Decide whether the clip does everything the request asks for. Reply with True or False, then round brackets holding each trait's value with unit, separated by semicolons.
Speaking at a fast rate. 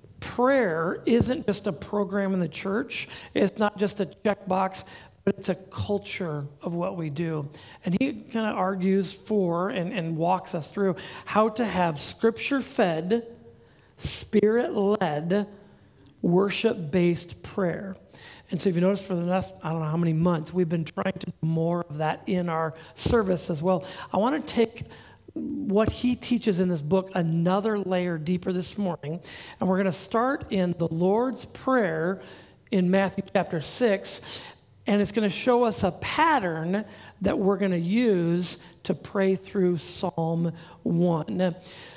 False (165 wpm)